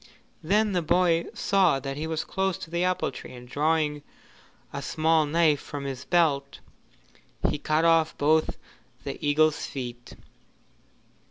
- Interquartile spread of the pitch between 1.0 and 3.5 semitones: Yes, average, 2.7 semitones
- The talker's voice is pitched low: No, medium, 155 Hz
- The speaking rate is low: No, average, 145 wpm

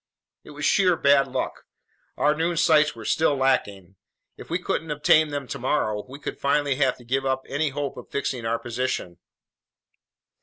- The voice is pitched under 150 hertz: Yes, medium, 140 Hz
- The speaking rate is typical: Yes, average, 175 wpm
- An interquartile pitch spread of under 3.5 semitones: Yes, average, 3.1 semitones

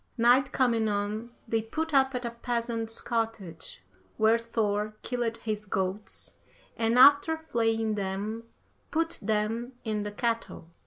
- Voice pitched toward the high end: Yes, high, 225 Hz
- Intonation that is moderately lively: No, narrow, 2.2 semitones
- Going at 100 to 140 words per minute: Yes, slow, 135 wpm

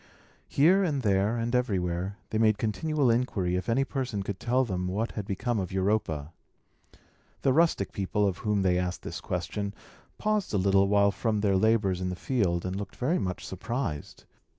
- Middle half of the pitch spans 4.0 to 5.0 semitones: Yes, average, 4.4 semitones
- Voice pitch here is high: No, low, 105 Hz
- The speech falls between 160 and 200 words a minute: Yes, average, 180 wpm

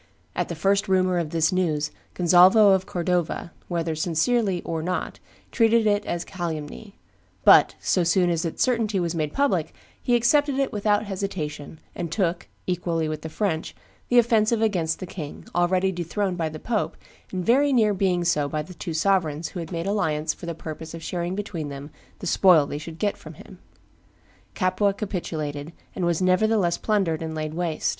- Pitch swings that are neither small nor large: Yes, average, 3.9 semitones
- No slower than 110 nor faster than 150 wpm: No, average, 180 wpm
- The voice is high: No, medium, 180 Hz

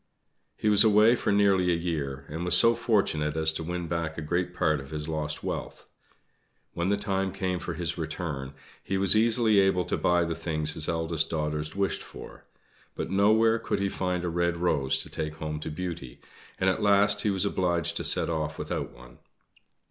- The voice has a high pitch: No, very low, 85 Hz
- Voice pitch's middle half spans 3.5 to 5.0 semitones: Yes, average, 3.8 semitones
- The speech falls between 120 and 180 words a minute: No, average, 200 wpm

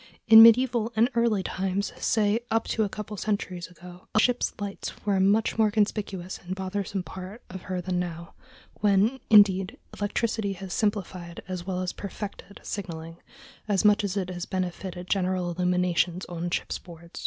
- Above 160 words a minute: Yes, average, 170 wpm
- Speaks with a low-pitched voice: No, high, 195 Hz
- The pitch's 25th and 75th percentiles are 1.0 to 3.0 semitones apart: Yes, average, 2.7 semitones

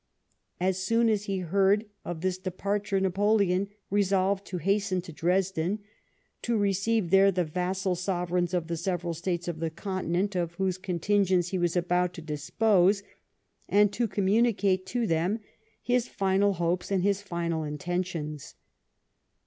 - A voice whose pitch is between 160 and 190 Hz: Yes, medium, 185 Hz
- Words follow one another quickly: No, average, 145 wpm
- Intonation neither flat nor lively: No, narrow, 2.3 semitones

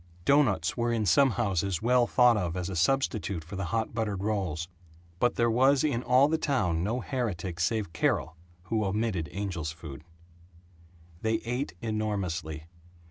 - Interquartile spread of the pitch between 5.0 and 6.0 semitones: Yes, wide, 5.5 semitones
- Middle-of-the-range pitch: No, low, 105 Hz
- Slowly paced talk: No, average, 155 wpm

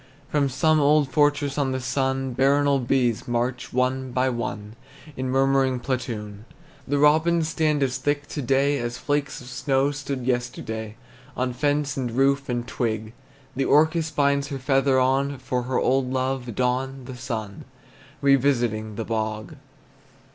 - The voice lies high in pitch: No, low, 130 Hz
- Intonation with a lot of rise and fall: No, narrow, 2.4 semitones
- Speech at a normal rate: Yes, average, 150 wpm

